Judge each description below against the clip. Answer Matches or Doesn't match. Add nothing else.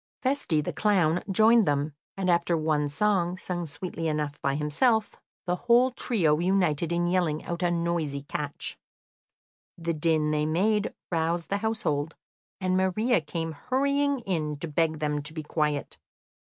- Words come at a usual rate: Matches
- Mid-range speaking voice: Matches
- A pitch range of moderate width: Matches